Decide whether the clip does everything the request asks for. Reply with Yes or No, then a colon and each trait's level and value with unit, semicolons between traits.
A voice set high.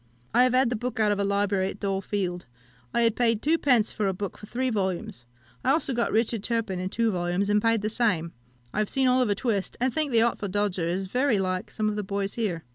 Yes: high, 210 Hz